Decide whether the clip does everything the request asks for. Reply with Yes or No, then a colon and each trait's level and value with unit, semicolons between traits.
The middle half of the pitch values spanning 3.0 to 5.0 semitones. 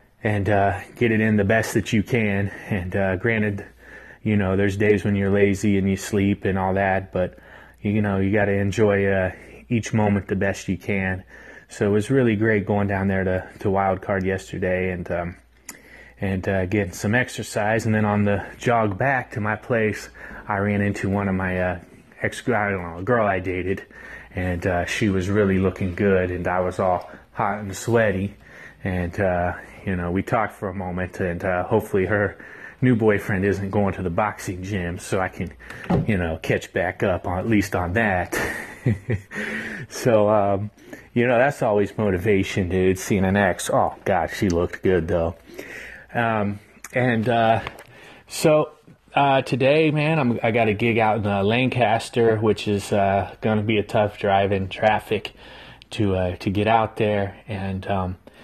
No: narrow, 2.4 semitones